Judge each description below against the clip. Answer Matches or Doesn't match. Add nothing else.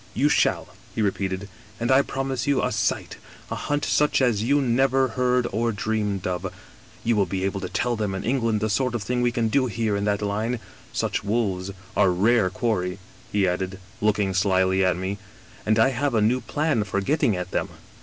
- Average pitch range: Matches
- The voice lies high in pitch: Doesn't match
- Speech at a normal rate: Doesn't match